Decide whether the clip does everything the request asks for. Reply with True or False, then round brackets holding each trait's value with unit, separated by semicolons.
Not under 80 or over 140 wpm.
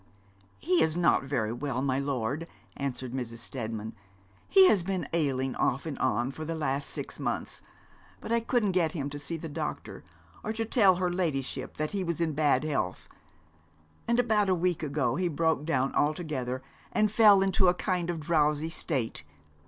False (180 wpm)